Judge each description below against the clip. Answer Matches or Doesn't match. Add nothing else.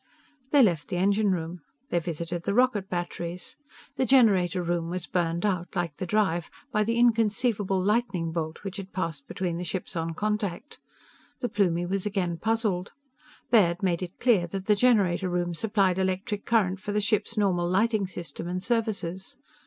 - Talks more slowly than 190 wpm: Matches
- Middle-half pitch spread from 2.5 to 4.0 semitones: Matches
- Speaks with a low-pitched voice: Doesn't match